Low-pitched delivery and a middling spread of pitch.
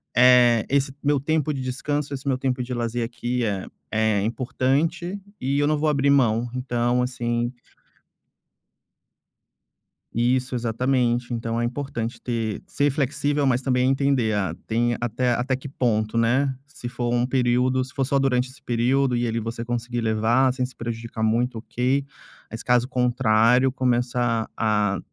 No: low, 125 Hz; narrow, 2.2 semitones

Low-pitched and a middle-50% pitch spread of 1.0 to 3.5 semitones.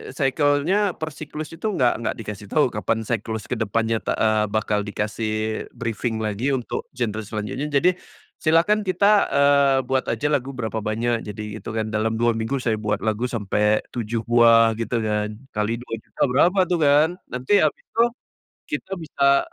No: low, 115 Hz; average, 4.7 semitones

